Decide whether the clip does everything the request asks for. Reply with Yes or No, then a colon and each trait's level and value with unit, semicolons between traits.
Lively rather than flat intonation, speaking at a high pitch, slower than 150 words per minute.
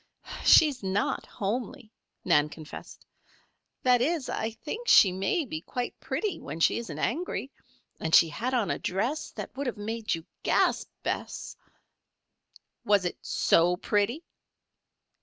Yes: wide, 5.8 semitones; high, 225 Hz; average, 140 wpm